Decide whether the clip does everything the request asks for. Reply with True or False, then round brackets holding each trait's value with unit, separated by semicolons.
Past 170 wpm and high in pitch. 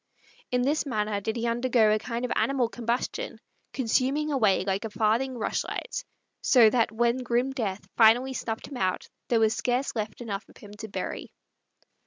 True (180 wpm; 235 Hz)